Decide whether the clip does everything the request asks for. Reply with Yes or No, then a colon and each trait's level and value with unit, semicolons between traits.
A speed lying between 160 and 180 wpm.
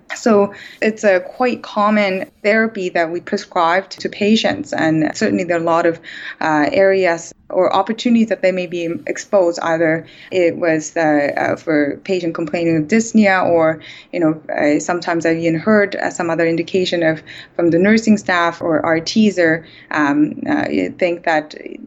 Yes: average, 175 wpm